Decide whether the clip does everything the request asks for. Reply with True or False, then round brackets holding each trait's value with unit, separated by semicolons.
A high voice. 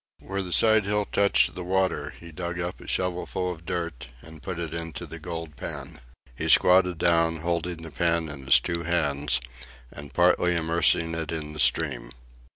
False (85 Hz)